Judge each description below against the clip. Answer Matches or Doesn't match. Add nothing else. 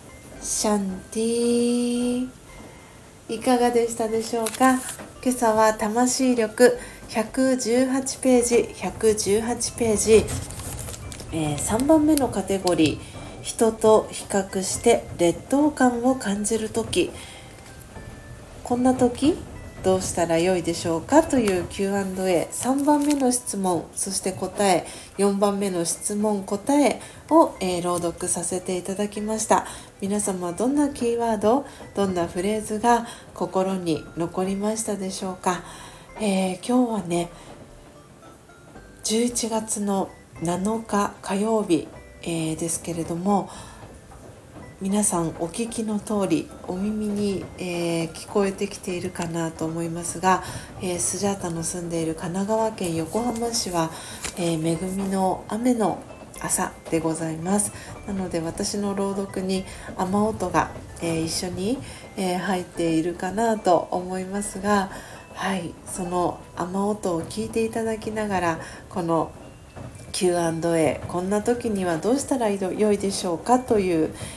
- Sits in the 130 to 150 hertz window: Doesn't match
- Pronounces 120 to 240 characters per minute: Matches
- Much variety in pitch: Doesn't match